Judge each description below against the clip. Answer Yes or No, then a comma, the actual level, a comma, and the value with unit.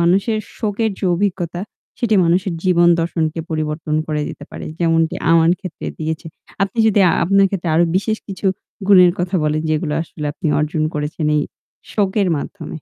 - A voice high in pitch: No, medium, 170 Hz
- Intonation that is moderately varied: Yes, average, 3.8 semitones